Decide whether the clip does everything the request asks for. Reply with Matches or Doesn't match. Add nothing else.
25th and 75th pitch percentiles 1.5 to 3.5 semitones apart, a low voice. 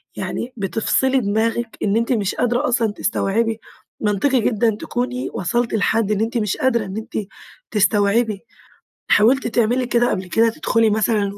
Doesn't match